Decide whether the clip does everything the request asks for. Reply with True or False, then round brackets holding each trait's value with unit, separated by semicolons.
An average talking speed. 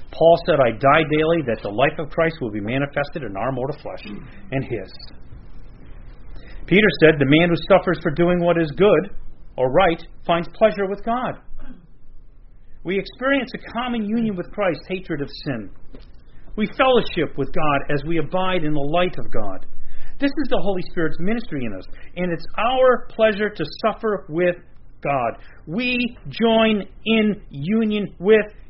True (165 wpm)